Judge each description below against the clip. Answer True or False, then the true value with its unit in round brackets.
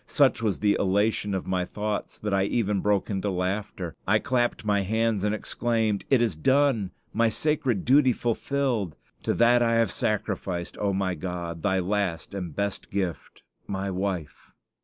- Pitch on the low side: True (105 Hz)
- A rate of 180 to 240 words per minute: False (170 wpm)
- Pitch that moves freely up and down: False (3.4 semitones)